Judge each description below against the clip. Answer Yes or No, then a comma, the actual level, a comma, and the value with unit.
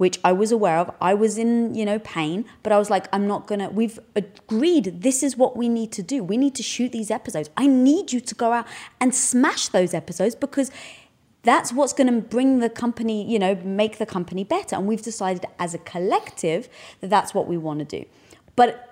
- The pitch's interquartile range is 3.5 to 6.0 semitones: Yes, average, 4.2 semitones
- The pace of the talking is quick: Yes, fast, 230 wpm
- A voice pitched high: Yes, high, 225 Hz